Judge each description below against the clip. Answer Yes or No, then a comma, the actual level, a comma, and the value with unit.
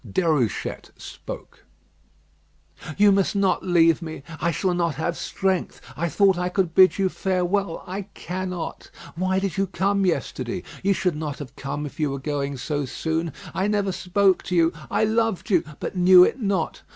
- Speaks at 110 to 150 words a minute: No, average, 175 wpm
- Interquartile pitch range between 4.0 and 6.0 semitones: No, average, 3.1 semitones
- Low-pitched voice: No, medium, 180 Hz